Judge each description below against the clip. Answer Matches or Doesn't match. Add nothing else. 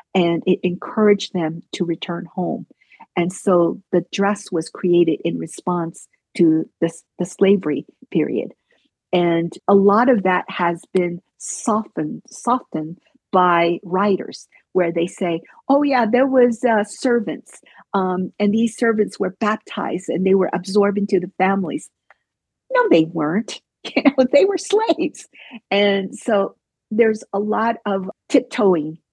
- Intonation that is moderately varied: Matches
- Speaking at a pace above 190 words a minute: Doesn't match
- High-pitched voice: Matches